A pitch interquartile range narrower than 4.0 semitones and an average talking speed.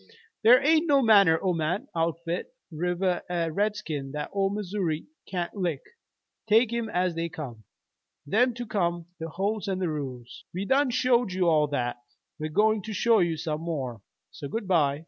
No: average, 5.2 semitones; average, 175 wpm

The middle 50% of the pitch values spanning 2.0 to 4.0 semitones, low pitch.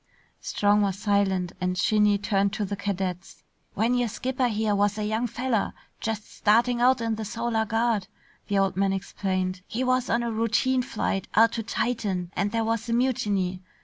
No: average, 2.8 semitones; high, 210 Hz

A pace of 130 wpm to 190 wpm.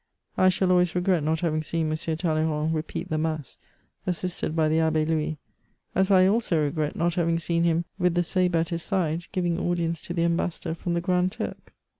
No: average, 200 wpm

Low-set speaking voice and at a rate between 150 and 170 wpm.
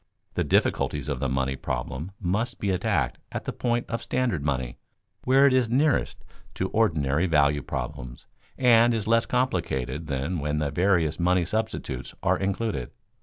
Yes: very low, 90 Hz; average, 160 wpm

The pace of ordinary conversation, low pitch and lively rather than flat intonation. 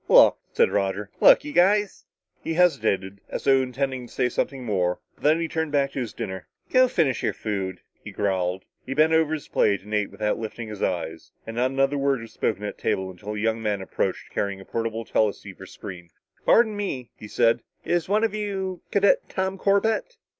No: fast, 210 wpm; low, 125 Hz; wide, 7.9 semitones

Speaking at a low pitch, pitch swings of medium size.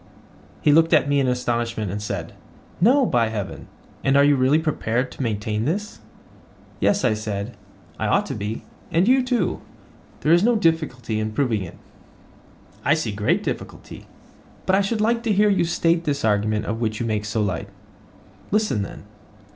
No: low, 130 Hz; wide, 7.8 semitones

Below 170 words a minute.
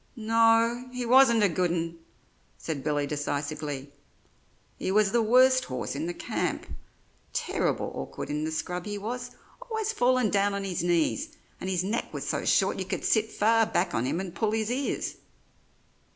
No: average, 175 wpm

